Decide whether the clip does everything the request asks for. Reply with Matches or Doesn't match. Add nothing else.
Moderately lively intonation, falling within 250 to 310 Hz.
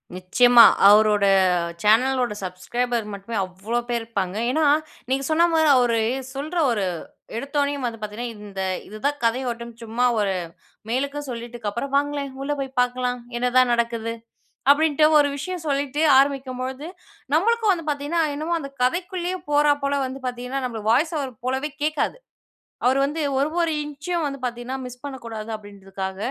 Matches